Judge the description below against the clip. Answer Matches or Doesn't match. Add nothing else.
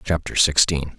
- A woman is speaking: Doesn't match